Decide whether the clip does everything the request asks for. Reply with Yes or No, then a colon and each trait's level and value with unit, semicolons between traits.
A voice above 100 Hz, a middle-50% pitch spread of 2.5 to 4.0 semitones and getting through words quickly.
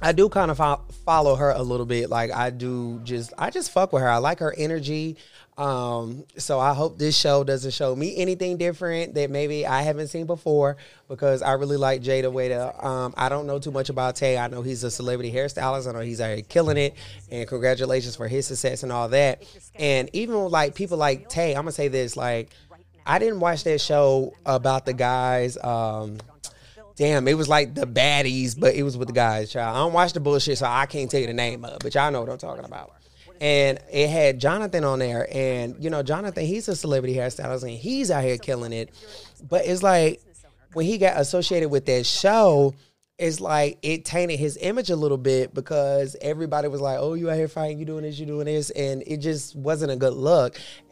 Yes: medium, 140 Hz; average, 3.4 semitones; fast, 225 wpm